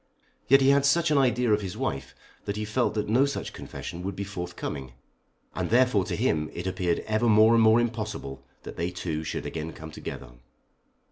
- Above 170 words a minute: Yes, average, 200 wpm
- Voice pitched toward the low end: Yes, low, 105 Hz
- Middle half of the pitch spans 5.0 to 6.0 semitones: Yes, wide, 5.4 semitones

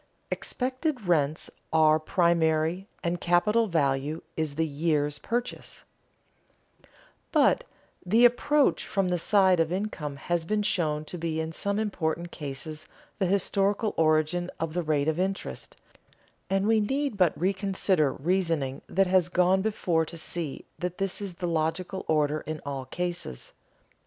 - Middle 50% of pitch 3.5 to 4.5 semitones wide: Yes, average, 3.8 semitones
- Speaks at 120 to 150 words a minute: Yes, average, 145 wpm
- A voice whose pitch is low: No, medium, 175 Hz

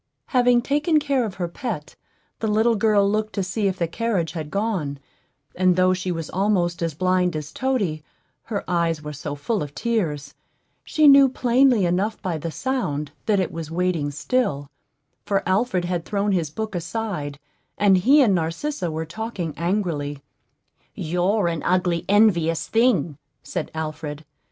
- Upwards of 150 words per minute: Yes, average, 160 wpm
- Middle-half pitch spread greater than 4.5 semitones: Yes, average, 5.3 semitones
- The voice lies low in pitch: No, medium, 185 Hz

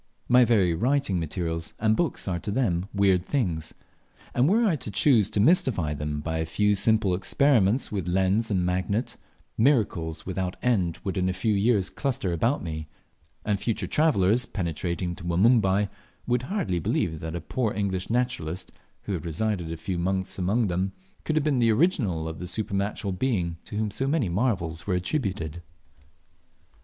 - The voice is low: Yes, low, 100 Hz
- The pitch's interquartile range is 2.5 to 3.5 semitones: No, average, 5.2 semitones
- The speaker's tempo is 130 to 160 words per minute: No, average, 175 wpm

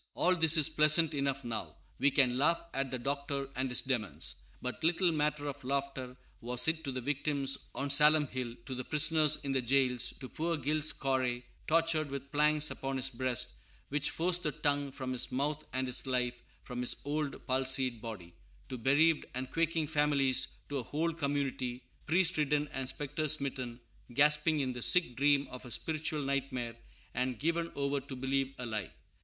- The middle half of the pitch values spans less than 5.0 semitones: Yes, average, 2.8 semitones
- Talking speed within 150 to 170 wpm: No, average, 185 wpm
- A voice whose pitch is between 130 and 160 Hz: Yes, medium, 140 Hz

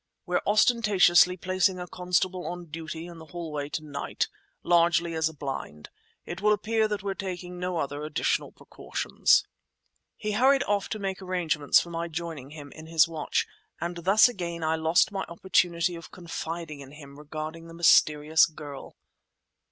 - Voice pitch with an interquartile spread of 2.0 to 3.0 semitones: Yes, average, 2.7 semitones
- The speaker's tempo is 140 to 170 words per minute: Yes, average, 160 wpm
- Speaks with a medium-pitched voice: Yes, medium, 170 Hz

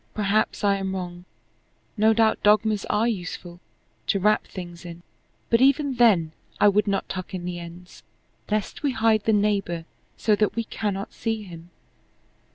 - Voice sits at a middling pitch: No, high, 205 Hz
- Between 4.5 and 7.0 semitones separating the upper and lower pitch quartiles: No, average, 3.5 semitones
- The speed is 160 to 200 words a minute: Yes, average, 165 wpm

